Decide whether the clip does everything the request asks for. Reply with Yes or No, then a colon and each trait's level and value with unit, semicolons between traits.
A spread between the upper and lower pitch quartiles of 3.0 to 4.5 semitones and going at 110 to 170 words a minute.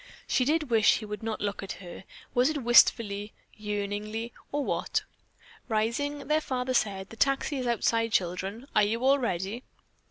Yes: average, 3.9 semitones; average, 165 wpm